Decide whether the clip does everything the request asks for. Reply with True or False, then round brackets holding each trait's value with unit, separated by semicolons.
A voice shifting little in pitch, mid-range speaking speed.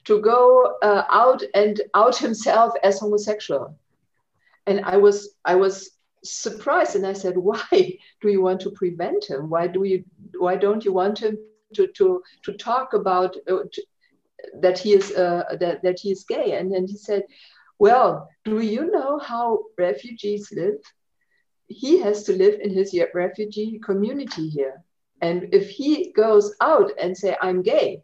False (4.2 semitones; 165 wpm)